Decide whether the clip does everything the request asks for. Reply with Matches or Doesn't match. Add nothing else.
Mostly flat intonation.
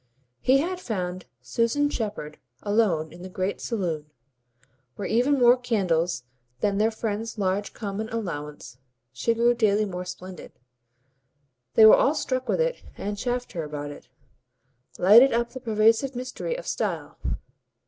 Doesn't match